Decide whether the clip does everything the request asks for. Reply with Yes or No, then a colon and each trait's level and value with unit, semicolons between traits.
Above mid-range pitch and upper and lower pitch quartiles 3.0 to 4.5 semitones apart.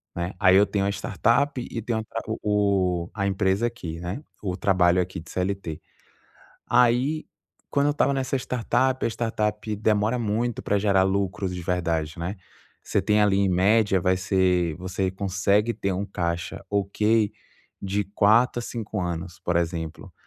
No: low, 100 Hz; average, 3.3 semitones